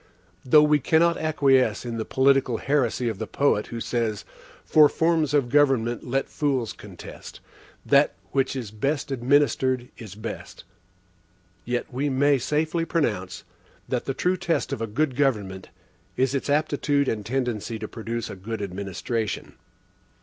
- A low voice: Yes, low, 130 Hz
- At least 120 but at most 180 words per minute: Yes, average, 150 wpm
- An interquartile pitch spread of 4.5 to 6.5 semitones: No, average, 4.1 semitones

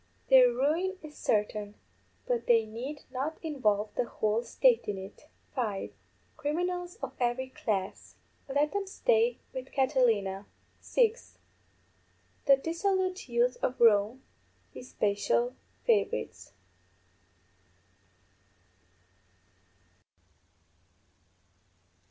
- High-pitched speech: Yes, very high, 260 Hz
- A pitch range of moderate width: No, wide, 8.0 semitones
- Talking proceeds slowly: Yes, slow, 90 wpm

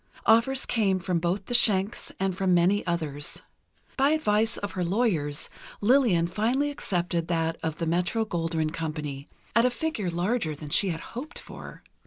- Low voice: No, medium, 185 Hz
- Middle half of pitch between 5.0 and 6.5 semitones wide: Yes, wide, 5.5 semitones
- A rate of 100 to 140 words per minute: No, average, 165 wpm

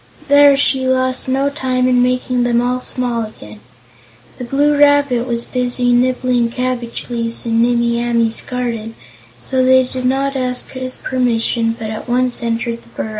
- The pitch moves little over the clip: Yes, narrow, 1.7 semitones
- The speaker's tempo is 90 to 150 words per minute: No, average, 165 wpm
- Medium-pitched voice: No, very high, 250 Hz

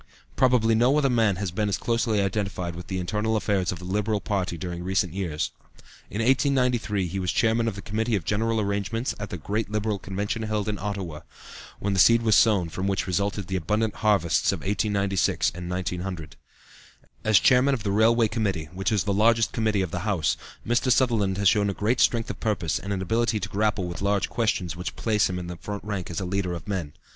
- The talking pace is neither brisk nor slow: No, fast, 210 wpm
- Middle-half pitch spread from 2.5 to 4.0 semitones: Yes, average, 3.1 semitones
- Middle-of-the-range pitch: No, low, 100 Hz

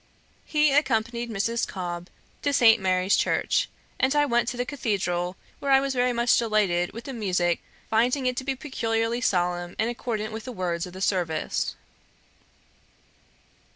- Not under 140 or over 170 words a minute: Yes, average, 160 wpm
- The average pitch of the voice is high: Yes, high, 225 Hz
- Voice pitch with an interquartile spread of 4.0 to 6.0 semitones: Yes, average, 5.3 semitones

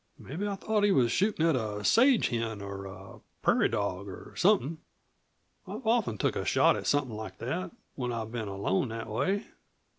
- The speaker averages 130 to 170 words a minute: No, average, 185 wpm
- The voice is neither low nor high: No, low, 120 Hz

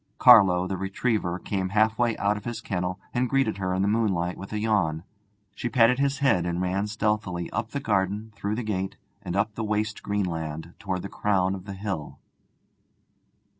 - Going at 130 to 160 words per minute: No, average, 190 wpm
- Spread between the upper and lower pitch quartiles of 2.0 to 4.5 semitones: Yes, average, 3.0 semitones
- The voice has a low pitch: Yes, low, 100 Hz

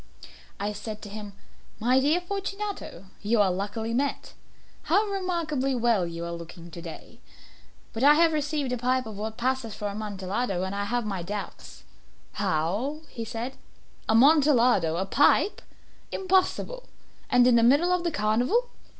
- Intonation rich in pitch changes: Yes, wide, 6.7 semitones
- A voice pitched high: Yes, high, 235 Hz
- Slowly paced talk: No, average, 155 wpm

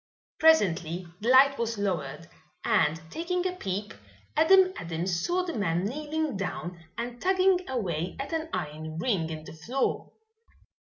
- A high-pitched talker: Yes, high, 220 Hz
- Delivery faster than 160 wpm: No, average, 145 wpm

